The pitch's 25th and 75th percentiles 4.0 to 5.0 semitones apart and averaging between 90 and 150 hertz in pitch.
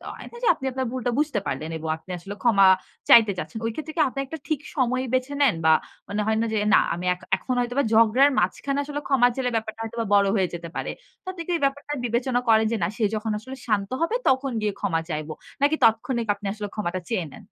No: average, 4.7 semitones; high, 230 Hz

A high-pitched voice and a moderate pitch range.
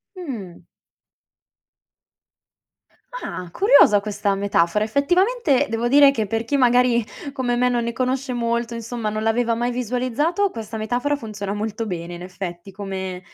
Yes: high, 230 Hz; average, 3.7 semitones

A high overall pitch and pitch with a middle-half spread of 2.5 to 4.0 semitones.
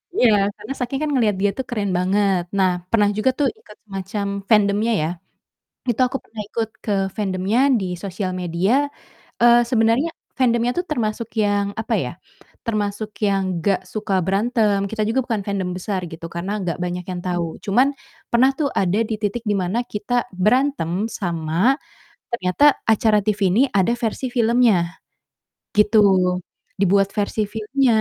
Yes: high, 210 Hz; average, 3.3 semitones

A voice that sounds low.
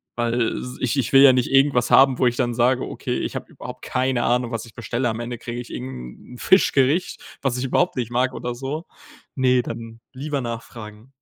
Yes: low, 125 Hz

